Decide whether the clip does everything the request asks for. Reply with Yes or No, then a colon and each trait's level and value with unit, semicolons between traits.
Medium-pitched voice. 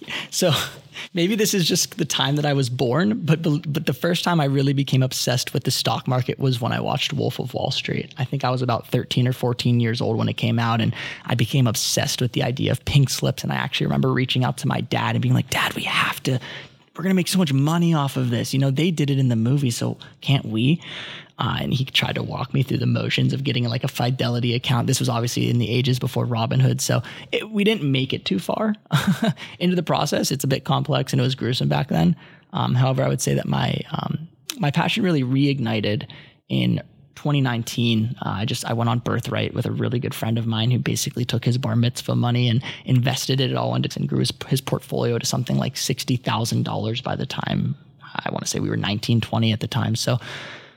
No: low, 130 Hz